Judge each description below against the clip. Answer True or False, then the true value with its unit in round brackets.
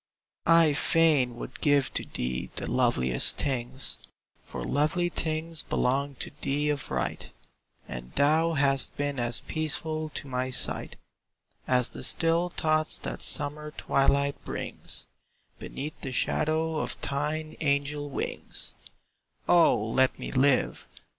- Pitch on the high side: False (145 Hz)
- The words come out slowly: True (125 wpm)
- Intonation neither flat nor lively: True (3.2 semitones)